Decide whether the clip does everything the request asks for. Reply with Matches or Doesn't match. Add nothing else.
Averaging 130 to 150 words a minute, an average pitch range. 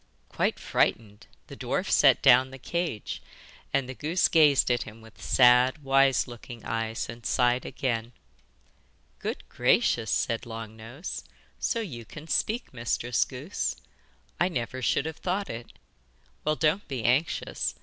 Matches